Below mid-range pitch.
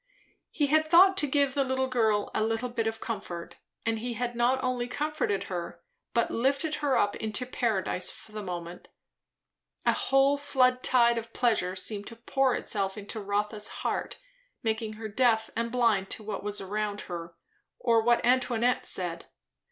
No: high, 230 Hz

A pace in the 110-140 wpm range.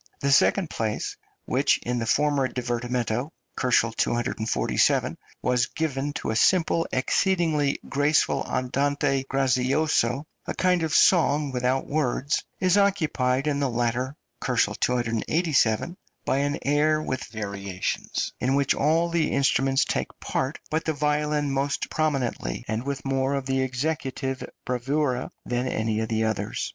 Yes: slow, 135 wpm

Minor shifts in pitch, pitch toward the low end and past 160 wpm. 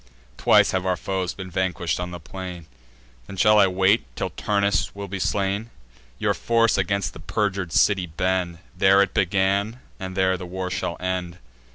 Yes: narrow, 1.7 semitones; very low, 95 Hz; average, 175 wpm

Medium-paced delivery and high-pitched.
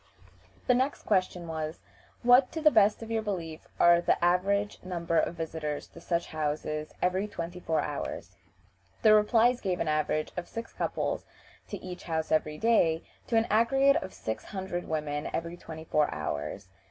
No: average, 170 wpm; medium, 175 Hz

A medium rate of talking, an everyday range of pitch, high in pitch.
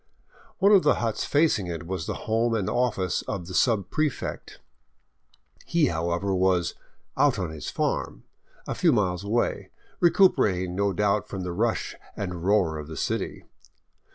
No: average, 165 wpm; average, 4.7 semitones; low, 100 Hz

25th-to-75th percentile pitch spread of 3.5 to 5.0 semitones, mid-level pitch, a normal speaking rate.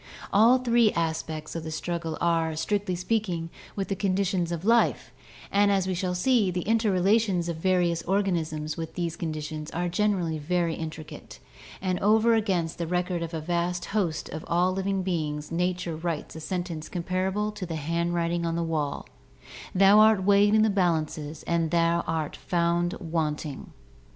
No: average, 3.0 semitones; medium, 175 Hz; average, 160 wpm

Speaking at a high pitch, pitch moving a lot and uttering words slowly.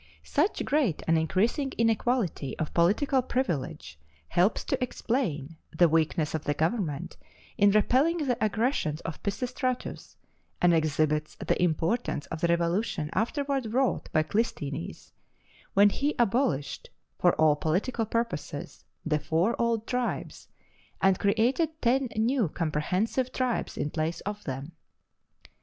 Yes: high, 200 Hz; wide, 7.7 semitones; slow, 125 wpm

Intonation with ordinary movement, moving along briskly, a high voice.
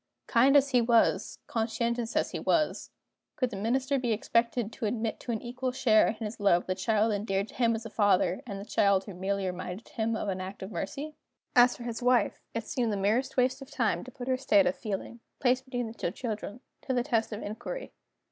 Yes: average, 3.4 semitones; fast, 225 wpm; high, 230 Hz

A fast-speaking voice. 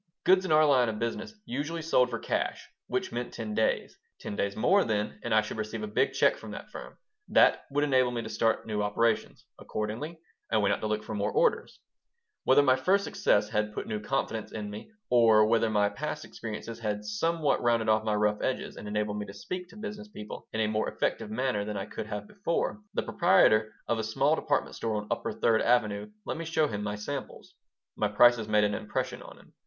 Yes: fast, 225 wpm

